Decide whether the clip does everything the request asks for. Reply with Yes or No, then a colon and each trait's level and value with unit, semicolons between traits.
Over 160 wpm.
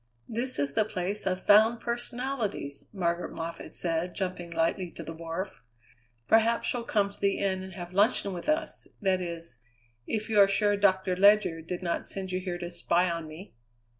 Yes: average, 185 wpm